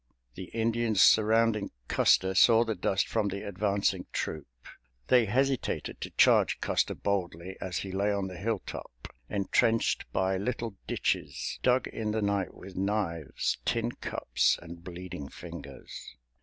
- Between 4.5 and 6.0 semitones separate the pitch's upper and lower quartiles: No, average, 3.3 semitones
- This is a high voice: No, low, 100 Hz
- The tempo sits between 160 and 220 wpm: No, average, 140 wpm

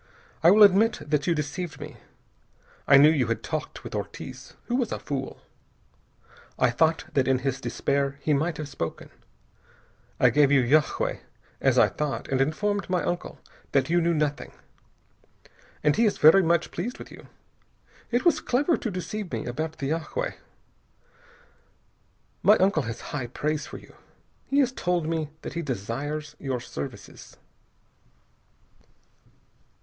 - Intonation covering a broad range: No, average, 4.7 semitones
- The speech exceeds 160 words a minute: No, average, 155 wpm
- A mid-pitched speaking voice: Yes, medium, 155 Hz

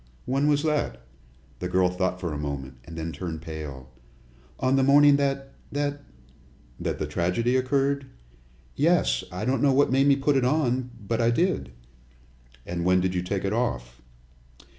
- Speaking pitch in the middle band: No, low, 105 Hz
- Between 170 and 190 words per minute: Yes, average, 175 wpm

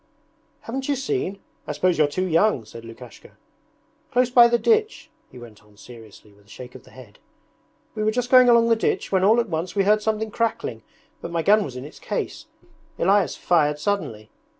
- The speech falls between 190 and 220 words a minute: Yes, average, 200 wpm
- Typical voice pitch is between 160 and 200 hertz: Yes, high, 190 Hz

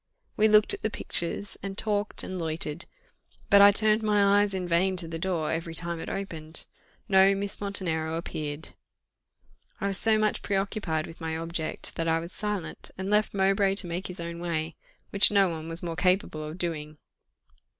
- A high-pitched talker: No, medium, 180 Hz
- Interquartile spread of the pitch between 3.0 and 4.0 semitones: Yes, average, 3.5 semitones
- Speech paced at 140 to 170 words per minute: No, average, 185 wpm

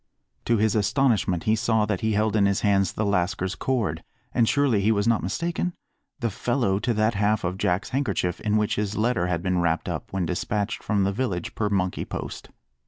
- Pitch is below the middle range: Yes, low, 105 Hz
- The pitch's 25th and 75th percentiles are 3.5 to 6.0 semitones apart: No, average, 2.8 semitones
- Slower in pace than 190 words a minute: No, fast, 205 wpm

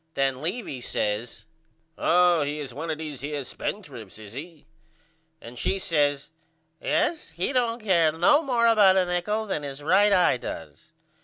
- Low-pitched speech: No, medium, 160 Hz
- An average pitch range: No, wide, 6.3 semitones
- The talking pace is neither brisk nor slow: Yes, average, 160 wpm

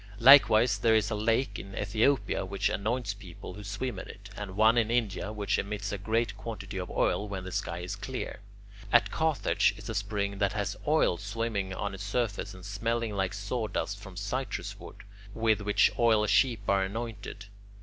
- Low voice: Yes, low, 105 Hz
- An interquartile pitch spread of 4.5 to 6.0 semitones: No, narrow, 2.4 semitones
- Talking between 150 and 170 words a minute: No, average, 185 wpm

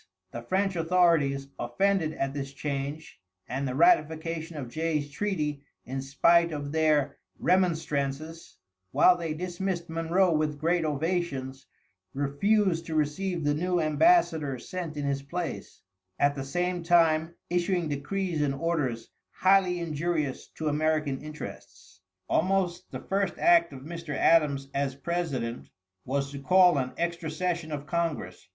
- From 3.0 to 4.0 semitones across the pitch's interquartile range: Yes, average, 3.6 semitones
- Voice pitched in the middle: Yes, medium, 160 Hz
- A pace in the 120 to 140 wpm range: Yes, slow, 135 wpm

